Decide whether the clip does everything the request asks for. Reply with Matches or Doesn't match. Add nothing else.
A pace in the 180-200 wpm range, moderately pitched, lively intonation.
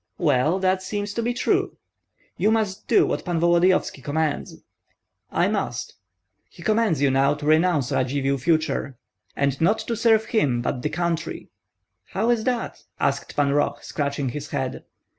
Doesn't match